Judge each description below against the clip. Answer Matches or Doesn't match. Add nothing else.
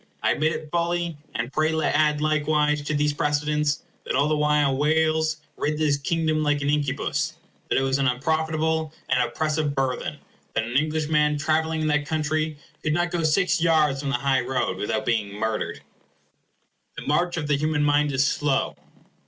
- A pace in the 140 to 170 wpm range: Doesn't match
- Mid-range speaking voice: Matches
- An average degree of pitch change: Doesn't match